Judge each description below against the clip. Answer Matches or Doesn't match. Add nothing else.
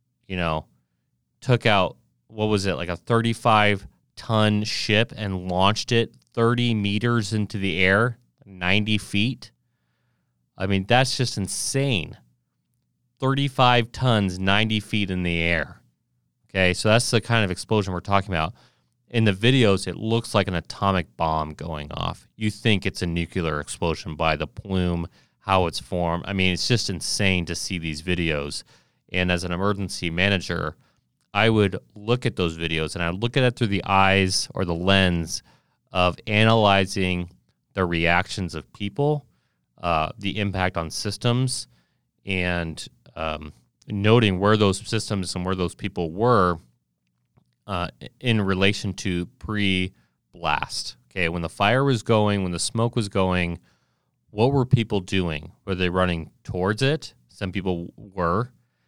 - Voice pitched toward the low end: Matches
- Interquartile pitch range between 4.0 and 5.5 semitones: Matches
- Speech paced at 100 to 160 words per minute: Matches